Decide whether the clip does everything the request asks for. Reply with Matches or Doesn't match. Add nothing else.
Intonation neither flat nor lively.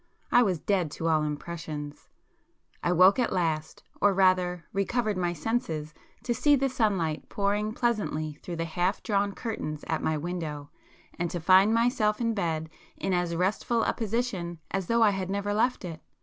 Matches